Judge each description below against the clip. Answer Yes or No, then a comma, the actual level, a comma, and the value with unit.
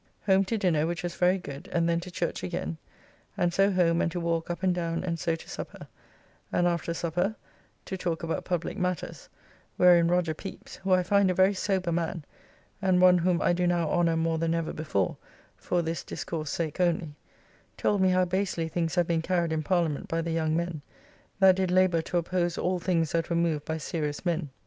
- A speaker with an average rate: No, fast, 210 wpm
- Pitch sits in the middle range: Yes, medium, 170 Hz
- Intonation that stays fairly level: Yes, narrow, 1.7 semitones